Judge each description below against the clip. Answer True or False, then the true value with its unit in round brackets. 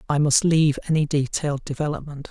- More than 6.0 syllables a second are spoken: True (6.4 syllables/s)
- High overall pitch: False (150 Hz)